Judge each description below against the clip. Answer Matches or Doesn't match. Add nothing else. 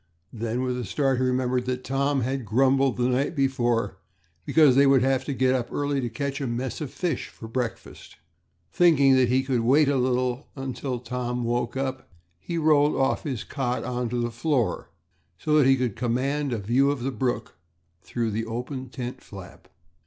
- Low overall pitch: Matches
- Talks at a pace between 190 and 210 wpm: Matches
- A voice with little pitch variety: Matches